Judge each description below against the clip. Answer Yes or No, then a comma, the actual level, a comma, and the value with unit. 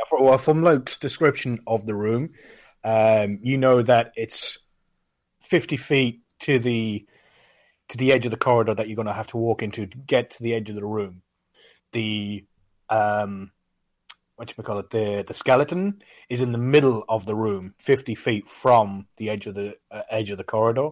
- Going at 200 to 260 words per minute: No, average, 190 wpm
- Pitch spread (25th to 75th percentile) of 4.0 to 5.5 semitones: No, average, 3.5 semitones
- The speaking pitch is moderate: No, low, 110 Hz